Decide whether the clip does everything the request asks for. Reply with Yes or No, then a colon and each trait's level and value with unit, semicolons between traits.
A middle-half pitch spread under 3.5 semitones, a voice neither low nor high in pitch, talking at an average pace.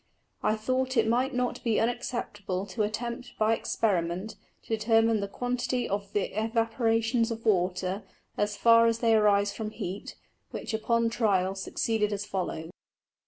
No: narrow, 2.4 semitones; high, 220 Hz; average, 150 wpm